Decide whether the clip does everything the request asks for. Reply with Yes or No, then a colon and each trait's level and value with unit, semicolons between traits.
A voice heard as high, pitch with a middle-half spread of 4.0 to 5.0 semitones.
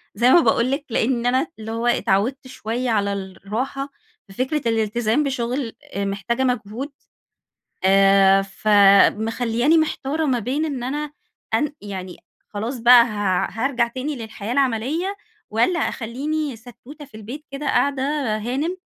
Yes: high, 240 Hz; average, 4.3 semitones